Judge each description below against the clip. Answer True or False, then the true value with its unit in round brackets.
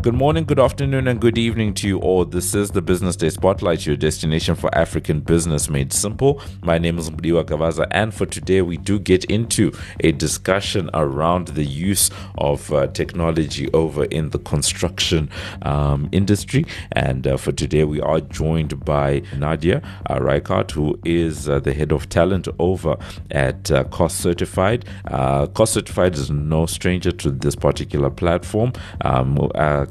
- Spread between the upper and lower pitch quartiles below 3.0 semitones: False (4.2 semitones)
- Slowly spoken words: False (170 wpm)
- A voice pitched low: True (85 Hz)